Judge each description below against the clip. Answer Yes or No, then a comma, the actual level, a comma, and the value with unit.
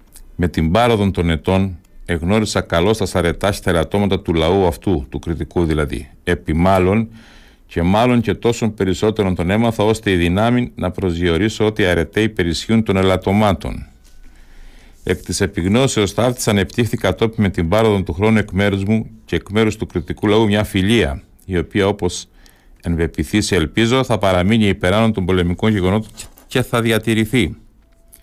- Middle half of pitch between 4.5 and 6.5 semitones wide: No, average, 3.6 semitones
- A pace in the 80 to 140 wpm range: No, average, 155 wpm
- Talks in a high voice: No, very low, 95 Hz